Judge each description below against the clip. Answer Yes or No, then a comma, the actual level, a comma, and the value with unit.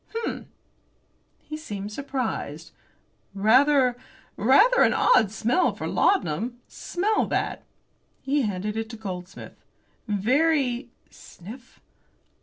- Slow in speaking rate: Yes, slow, 95 wpm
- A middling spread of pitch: No, wide, 5.7 semitones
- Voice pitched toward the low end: No, high, 240 Hz